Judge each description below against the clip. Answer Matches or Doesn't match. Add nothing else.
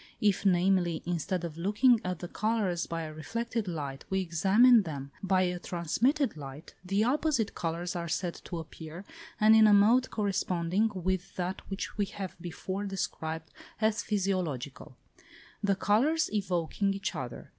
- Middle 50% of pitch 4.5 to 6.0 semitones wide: Doesn't match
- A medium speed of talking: Matches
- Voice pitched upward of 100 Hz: Matches